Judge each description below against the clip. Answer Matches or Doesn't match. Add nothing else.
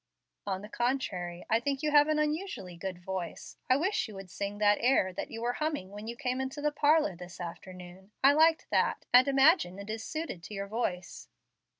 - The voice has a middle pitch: Doesn't match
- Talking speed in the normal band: Doesn't match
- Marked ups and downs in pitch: Matches